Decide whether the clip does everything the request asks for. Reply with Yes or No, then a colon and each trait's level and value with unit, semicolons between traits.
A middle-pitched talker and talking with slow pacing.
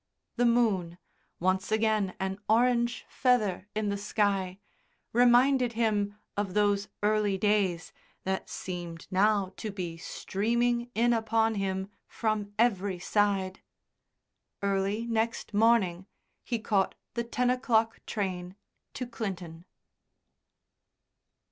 No: high, 210 Hz; slow, 110 wpm